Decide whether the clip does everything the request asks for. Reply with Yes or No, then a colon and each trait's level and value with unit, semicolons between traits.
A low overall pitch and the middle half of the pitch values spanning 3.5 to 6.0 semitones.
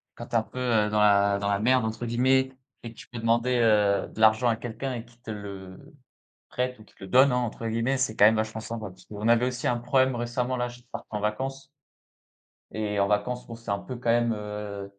No: low, 115 Hz; average, 2.8 semitones